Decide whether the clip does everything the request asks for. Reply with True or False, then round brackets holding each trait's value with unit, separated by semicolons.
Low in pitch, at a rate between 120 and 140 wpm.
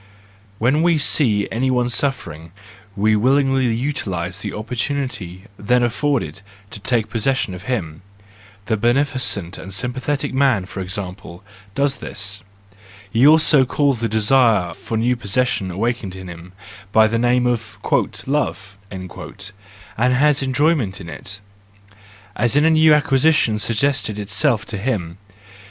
True (115 Hz; 135 wpm)